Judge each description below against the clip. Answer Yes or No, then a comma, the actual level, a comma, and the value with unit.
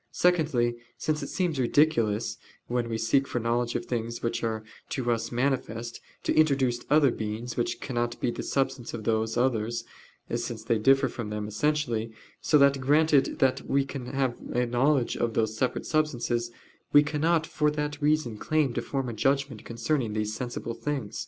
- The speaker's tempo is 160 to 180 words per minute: Yes, average, 170 wpm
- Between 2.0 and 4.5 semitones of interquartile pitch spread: Yes, average, 3.6 semitones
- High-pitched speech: No, low, 120 Hz